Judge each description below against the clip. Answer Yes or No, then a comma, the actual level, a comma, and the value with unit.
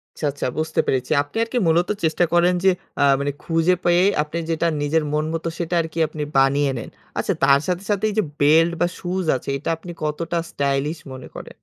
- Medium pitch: Yes, medium, 160 Hz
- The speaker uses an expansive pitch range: No, average, 3.3 semitones